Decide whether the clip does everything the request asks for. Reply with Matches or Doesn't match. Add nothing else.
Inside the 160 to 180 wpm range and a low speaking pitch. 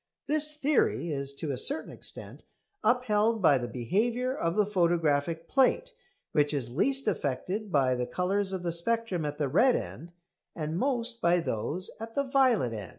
Doesn't match